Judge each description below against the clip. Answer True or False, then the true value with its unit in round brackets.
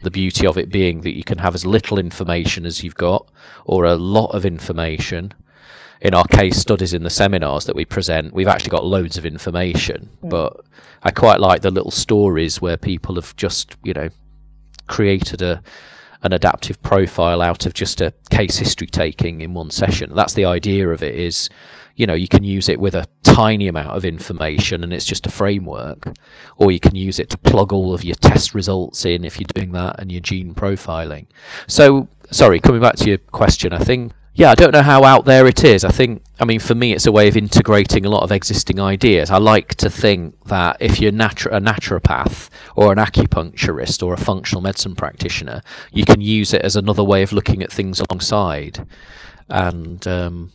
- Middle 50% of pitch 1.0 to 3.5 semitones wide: True (3.1 semitones)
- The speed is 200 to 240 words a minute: True (205 wpm)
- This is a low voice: True (95 Hz)